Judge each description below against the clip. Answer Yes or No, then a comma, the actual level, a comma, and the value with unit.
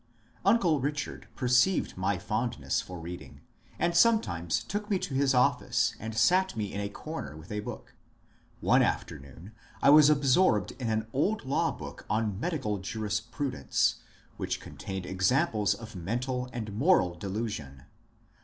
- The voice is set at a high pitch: No, low, 110 Hz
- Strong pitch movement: Yes, wide, 6.6 semitones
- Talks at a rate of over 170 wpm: No, average, 145 wpm